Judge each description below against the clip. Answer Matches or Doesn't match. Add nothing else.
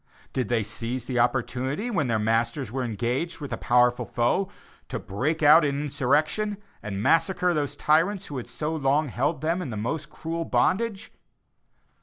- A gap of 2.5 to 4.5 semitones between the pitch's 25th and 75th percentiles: Doesn't match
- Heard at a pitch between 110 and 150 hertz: Matches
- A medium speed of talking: Matches